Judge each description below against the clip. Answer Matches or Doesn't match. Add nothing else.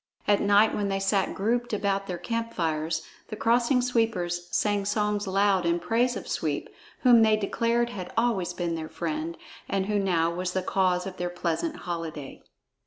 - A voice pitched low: Doesn't match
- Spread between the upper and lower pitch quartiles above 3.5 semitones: Matches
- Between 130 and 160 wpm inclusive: Doesn't match